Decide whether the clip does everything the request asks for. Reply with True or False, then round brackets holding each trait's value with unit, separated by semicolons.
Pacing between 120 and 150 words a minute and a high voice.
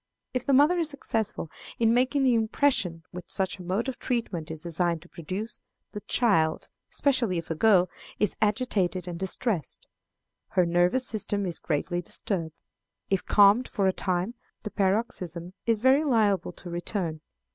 False (160 wpm; 195 Hz)